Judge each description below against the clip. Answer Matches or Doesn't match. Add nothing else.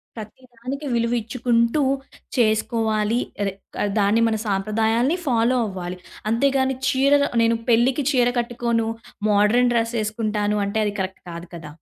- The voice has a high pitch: Matches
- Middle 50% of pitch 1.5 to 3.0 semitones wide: Matches